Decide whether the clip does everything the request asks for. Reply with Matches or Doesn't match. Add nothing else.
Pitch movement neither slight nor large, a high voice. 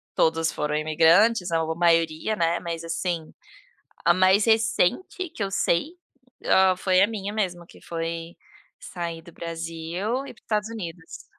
Doesn't match